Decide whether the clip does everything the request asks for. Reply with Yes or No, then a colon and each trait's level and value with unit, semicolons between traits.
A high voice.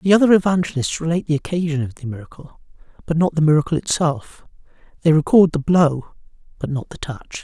No: medium, 155 Hz